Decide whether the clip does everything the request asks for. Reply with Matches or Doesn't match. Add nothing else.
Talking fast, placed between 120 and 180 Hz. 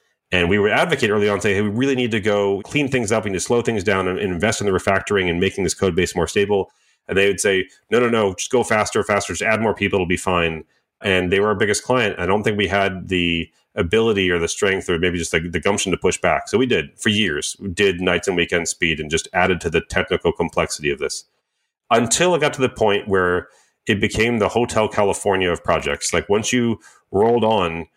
Doesn't match